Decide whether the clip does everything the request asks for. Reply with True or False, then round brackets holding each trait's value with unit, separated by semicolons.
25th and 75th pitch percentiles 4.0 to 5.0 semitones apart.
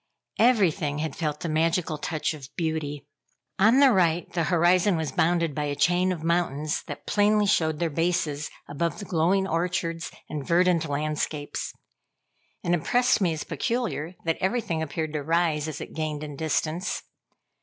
False (2.7 semitones)